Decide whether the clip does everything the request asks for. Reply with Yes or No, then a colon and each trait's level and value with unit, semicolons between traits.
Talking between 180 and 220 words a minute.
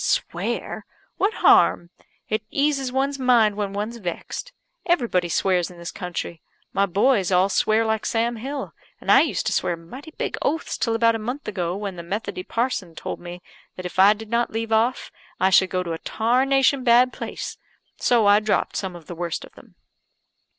Yes: average, 190 wpm